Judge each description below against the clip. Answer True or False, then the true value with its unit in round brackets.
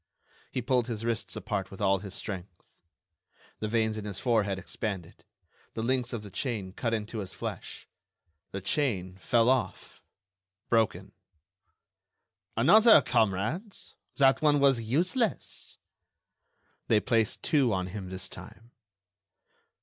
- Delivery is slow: True (125 wpm)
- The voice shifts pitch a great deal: False (4.5 semitones)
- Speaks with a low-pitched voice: True (110 Hz)